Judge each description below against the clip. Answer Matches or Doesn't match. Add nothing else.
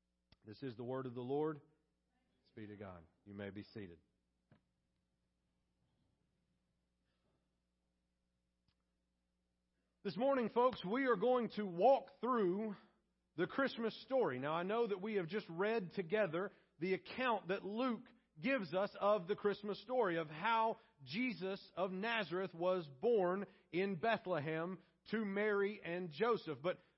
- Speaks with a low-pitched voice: Doesn't match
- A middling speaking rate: Doesn't match